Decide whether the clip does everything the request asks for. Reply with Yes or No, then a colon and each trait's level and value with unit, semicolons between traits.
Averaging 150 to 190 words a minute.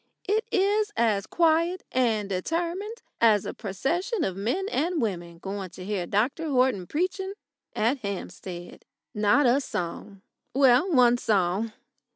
No: slow, 135 wpm